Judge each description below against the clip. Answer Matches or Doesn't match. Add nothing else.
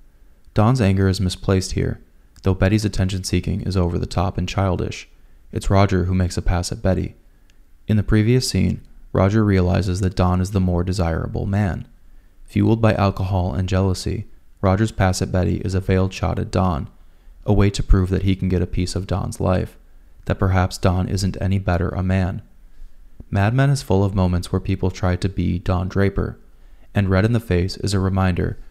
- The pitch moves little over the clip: Matches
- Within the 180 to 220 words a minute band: Matches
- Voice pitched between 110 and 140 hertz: Doesn't match